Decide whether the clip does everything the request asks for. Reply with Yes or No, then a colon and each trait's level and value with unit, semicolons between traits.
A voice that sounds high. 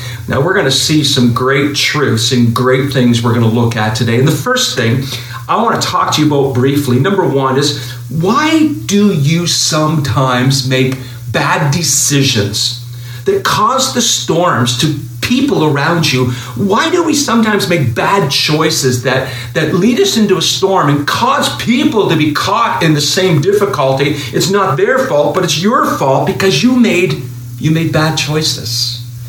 No: medium, 140 Hz